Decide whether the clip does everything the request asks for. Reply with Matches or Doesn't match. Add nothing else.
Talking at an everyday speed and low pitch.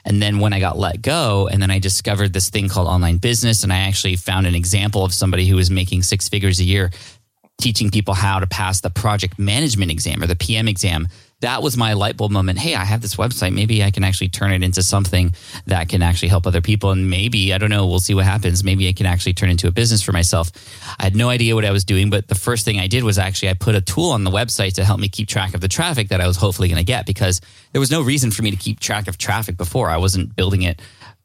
Doesn't match